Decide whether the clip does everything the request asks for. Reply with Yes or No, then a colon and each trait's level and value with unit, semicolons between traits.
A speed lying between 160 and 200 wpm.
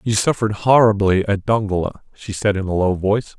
Yes: average, 195 wpm